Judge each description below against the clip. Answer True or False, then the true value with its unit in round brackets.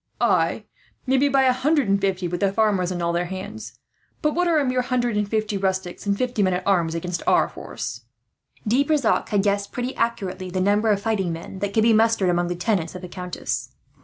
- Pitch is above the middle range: True (200 Hz)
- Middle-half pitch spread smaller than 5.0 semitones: True (4.3 semitones)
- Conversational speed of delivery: False (220 wpm)